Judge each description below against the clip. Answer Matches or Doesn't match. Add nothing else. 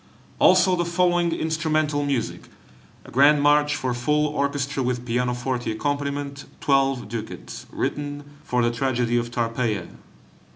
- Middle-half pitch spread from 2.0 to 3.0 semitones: Doesn't match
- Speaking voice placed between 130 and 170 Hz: Matches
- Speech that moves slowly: Matches